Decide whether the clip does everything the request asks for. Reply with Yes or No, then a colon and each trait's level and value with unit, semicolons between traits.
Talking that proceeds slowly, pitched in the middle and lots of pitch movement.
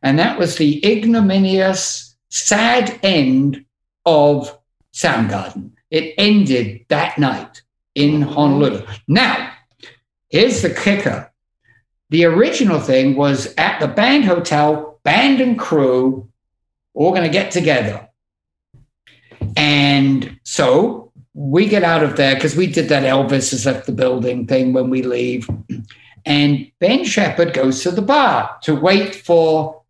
Yes: slow, 130 wpm; medium, 150 Hz; wide, 5.8 semitones